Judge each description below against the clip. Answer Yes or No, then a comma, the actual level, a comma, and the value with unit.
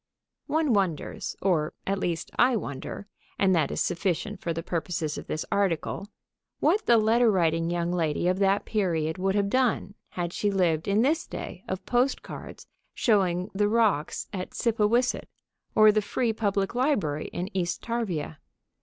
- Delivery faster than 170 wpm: No, average, 160 wpm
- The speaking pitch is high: Yes, high, 195 Hz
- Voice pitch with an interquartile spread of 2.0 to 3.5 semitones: No, average, 4.2 semitones